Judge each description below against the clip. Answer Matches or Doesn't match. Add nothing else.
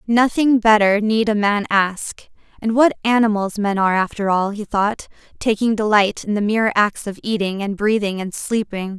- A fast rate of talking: Doesn't match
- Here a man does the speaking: Doesn't match